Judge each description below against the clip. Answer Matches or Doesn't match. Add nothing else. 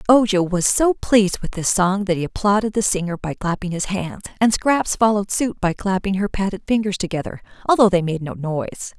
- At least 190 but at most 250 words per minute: Matches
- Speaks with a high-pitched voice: Matches